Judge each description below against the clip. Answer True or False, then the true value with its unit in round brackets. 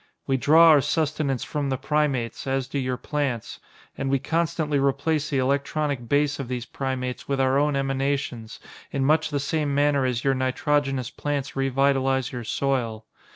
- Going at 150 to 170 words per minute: True (165 wpm)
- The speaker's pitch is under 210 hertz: True (135 Hz)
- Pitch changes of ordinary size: False (1.9 semitones)